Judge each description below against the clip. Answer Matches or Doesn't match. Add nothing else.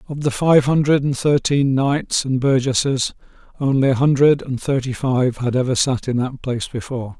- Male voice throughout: Matches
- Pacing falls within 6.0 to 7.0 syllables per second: Doesn't match